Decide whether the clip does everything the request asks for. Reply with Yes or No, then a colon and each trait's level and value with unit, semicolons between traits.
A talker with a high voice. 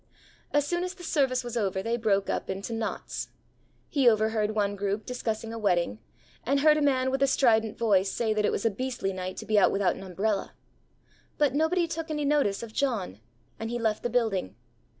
Yes: high, 225 Hz